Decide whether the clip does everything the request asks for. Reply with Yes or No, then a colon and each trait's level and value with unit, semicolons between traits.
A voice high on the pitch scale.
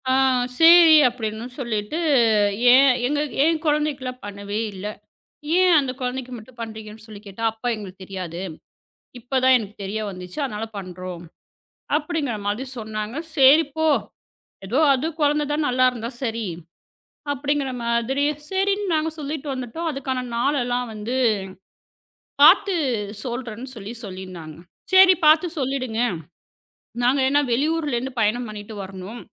Yes: high, 245 Hz